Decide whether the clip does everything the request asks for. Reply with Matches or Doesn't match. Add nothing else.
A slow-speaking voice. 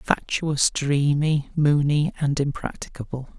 Matches